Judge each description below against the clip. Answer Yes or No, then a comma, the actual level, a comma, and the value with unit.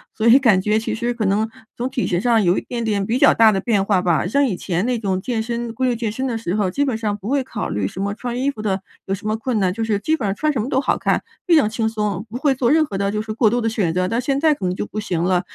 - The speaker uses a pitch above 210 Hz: Yes, high, 220 Hz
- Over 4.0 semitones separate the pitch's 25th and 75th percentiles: No, average, 3.6 semitones